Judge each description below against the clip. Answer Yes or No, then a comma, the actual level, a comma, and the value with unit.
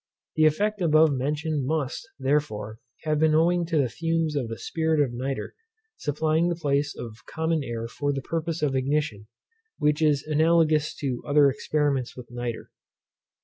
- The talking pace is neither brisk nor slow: Yes, average, 160 wpm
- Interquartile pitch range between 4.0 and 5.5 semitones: No, average, 3.1 semitones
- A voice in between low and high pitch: Yes, medium, 150 Hz